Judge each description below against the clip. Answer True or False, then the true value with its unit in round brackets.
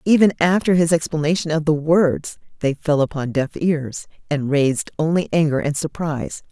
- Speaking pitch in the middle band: True (155 Hz)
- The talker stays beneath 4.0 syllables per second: False (5.0 syllables/s)